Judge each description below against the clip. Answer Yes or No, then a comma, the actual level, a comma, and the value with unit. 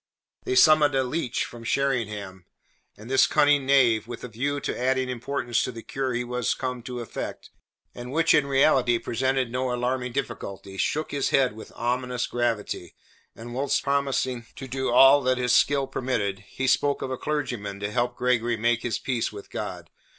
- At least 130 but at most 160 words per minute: No, average, 180 wpm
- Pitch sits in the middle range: No, low, 125 Hz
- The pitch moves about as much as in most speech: No, narrow, 2.3 semitones